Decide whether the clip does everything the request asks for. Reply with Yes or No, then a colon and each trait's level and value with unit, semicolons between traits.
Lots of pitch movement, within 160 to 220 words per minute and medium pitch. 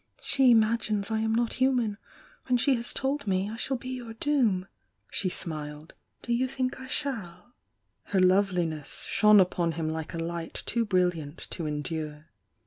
No: wide, 6.3 semitones; average, 170 wpm; high, 205 Hz